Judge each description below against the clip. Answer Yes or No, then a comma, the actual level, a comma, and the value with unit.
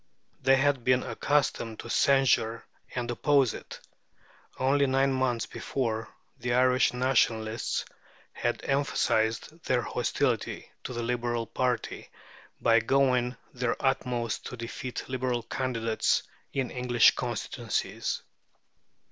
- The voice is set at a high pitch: No, low, 125 Hz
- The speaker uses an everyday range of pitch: No, narrow, 2.2 semitones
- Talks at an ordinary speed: No, slow, 110 wpm